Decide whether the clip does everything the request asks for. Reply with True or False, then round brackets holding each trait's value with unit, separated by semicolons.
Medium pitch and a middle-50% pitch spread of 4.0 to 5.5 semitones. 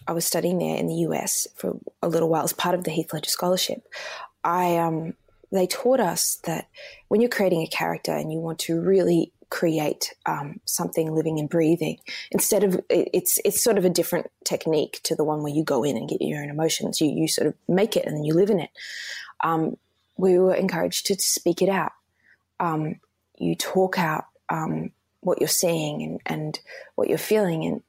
False (170 Hz; 3.1 semitones)